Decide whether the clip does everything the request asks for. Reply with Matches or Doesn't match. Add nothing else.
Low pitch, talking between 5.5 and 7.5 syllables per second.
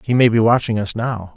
Matches